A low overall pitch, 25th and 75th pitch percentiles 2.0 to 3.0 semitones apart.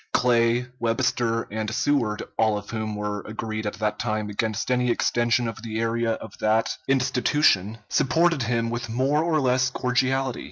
Yes: low, 115 Hz; narrow, 2.6 semitones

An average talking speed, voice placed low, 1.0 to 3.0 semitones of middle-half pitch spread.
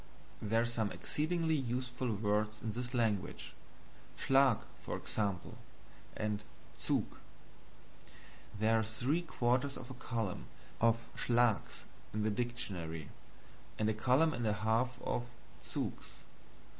No: slow, 120 wpm; low, 115 Hz; average, 2.7 semitones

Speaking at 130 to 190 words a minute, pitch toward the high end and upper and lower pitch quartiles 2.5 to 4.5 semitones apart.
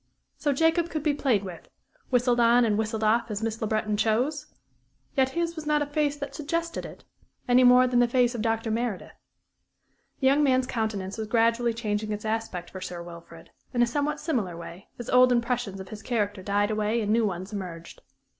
No: average, 200 wpm; high, 230 Hz; average, 3.7 semitones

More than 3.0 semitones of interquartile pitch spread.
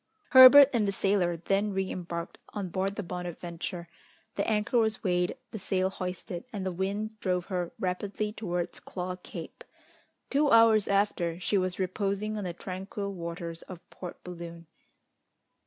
No: average, 2.7 semitones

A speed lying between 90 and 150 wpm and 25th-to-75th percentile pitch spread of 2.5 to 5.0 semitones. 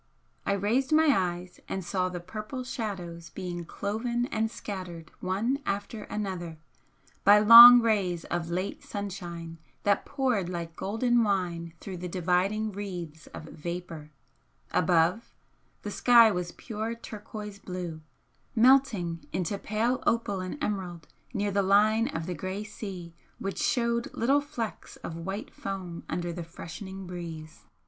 Yes: average, 140 wpm; average, 3.9 semitones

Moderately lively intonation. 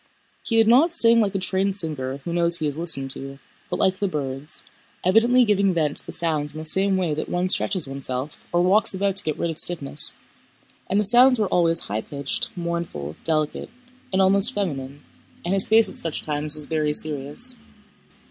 Yes: average, 4.9 semitones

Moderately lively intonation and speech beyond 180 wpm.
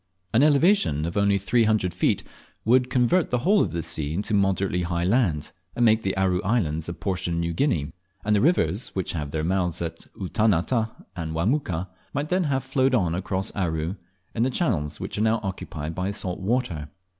No: wide, 6.2 semitones; average, 195 wpm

